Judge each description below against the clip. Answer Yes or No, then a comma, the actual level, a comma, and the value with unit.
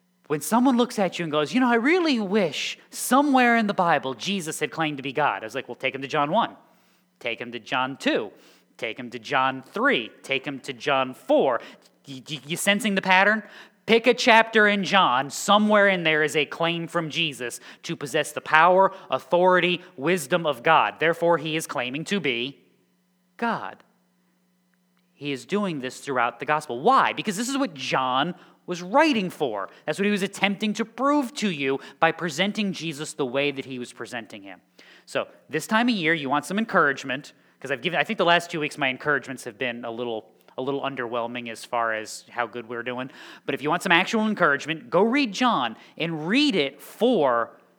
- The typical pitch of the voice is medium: Yes, medium, 160 Hz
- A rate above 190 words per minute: Yes, fast, 205 wpm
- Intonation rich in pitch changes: Yes, wide, 7.0 semitones